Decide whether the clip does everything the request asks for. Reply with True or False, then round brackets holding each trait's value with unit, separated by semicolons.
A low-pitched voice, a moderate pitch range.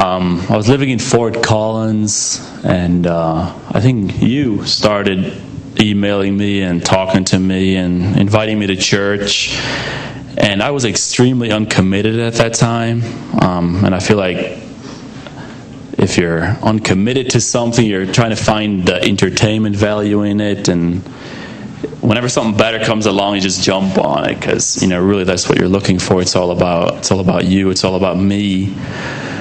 True (100 Hz; 3.3 semitones)